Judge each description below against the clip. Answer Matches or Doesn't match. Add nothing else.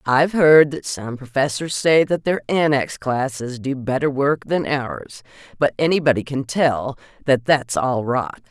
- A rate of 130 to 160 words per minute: Matches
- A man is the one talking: Doesn't match